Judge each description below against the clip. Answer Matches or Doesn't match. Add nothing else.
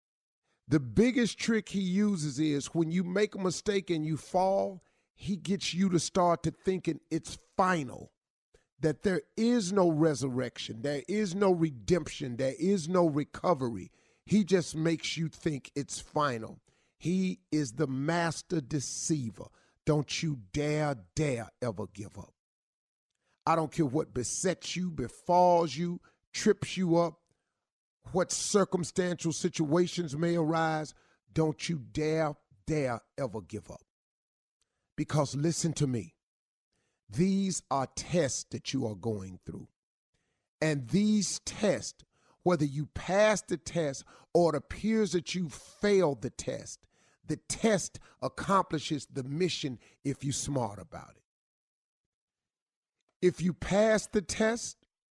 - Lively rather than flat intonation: Doesn't match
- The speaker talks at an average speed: Doesn't match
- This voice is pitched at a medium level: Matches